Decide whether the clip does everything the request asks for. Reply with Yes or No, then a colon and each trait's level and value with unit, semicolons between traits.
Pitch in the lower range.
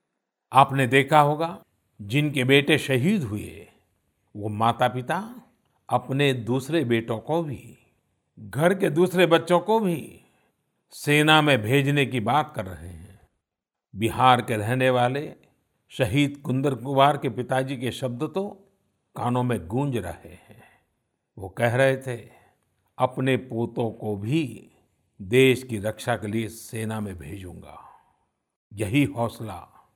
Yes: low, 125 Hz